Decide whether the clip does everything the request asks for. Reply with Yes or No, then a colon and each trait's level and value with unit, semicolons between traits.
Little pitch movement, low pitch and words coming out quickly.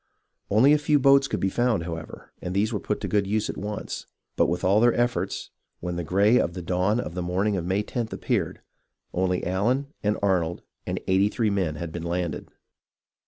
No: average, 3.8 semitones; low, 100 Hz; fast, 210 wpm